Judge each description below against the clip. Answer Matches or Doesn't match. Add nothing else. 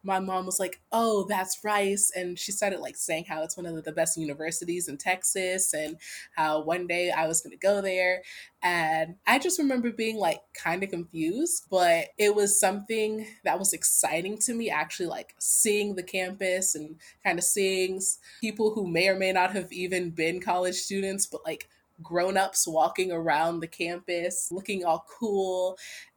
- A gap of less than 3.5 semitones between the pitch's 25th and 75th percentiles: Matches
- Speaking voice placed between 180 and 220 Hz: Matches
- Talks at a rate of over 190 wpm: Doesn't match